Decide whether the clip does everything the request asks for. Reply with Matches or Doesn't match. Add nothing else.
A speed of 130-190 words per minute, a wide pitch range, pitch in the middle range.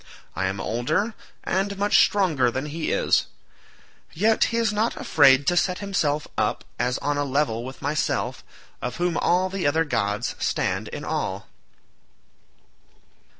Matches